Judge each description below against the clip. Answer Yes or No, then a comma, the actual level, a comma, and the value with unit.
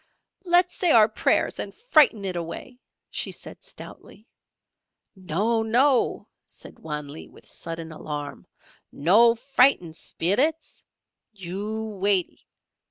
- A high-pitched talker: Yes, high, 210 Hz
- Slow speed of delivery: Yes, slow, 110 wpm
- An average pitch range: No, wide, 6.6 semitones